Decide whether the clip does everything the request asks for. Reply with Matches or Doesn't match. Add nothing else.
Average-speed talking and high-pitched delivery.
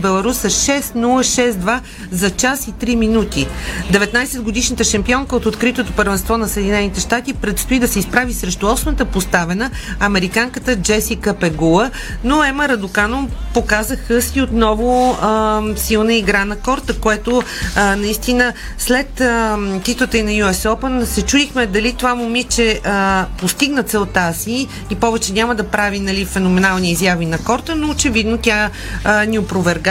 Matches